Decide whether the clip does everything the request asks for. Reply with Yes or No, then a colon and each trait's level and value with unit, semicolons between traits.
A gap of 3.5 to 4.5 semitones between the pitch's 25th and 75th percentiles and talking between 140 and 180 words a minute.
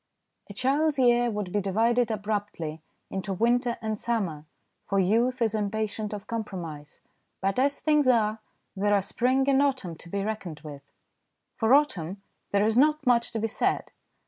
Yes: average, 4.0 semitones; average, 165 wpm